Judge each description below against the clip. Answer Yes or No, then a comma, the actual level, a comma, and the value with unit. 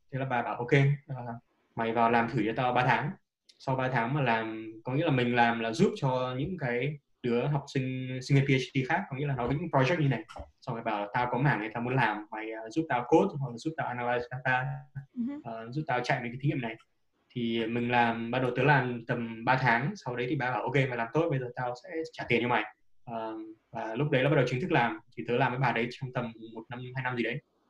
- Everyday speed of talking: No, fast, 275 wpm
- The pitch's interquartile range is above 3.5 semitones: No, average, 3.1 semitones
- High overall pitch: No, low, 125 Hz